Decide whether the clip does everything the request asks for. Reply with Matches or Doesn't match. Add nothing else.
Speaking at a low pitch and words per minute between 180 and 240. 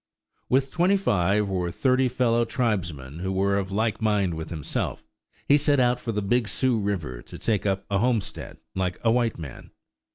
Matches